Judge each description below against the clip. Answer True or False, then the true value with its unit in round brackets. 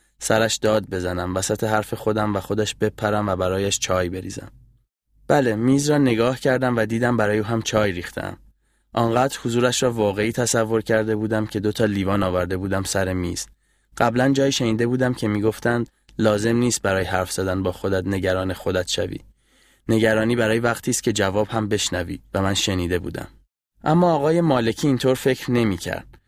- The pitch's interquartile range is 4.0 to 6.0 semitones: False (3.6 semitones)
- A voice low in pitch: True (110 Hz)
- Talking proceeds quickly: True (170 wpm)